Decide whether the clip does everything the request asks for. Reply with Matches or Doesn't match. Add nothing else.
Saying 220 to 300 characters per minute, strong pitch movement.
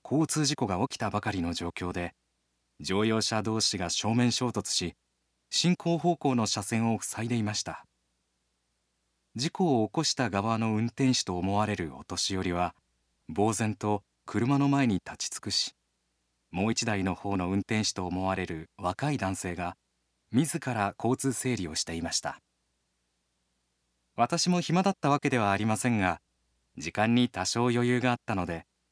Matches